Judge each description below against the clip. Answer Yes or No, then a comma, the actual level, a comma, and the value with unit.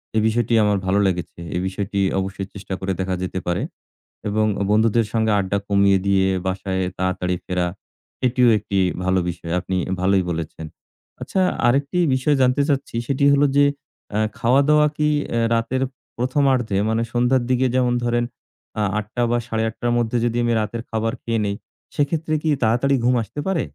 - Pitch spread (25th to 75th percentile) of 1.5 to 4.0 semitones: No, average, 4.7 semitones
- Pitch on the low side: Yes, low, 115 Hz